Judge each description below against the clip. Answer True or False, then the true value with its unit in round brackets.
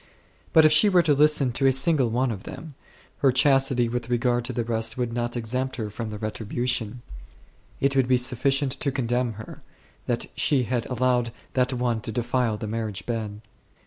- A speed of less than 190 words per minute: False (195 wpm)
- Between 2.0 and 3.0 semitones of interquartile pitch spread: True (2.6 semitones)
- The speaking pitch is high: False (125 Hz)